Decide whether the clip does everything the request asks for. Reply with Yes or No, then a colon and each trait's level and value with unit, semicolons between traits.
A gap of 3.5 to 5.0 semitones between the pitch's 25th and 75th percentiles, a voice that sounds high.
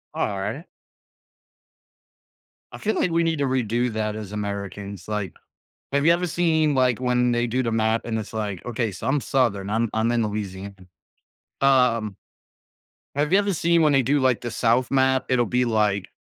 No: average, 4.3 semitones; low, 120 Hz